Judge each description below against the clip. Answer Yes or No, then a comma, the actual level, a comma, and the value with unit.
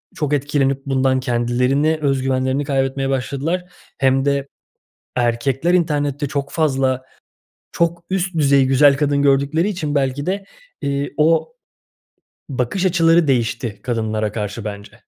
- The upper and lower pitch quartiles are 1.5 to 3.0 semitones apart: Yes, average, 2.7 semitones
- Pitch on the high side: No, medium, 140 Hz